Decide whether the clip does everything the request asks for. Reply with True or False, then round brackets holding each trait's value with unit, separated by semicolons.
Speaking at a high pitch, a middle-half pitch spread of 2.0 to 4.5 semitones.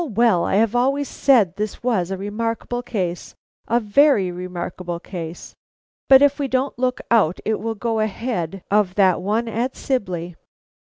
False (215 Hz; 5.0 semitones)